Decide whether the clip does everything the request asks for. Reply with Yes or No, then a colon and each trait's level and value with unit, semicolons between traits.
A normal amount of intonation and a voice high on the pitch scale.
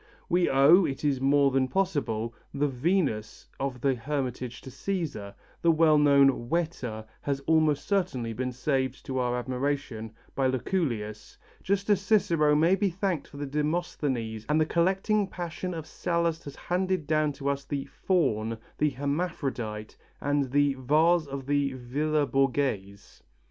No: average, 4.4 semitones; medium, 145 Hz